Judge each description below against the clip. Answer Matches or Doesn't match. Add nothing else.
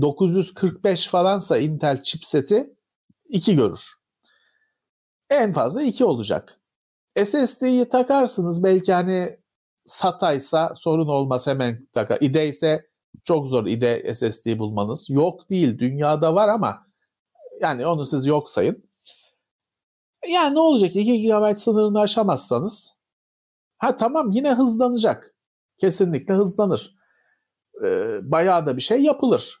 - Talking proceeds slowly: Doesn't match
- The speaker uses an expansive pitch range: Matches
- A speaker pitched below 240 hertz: Matches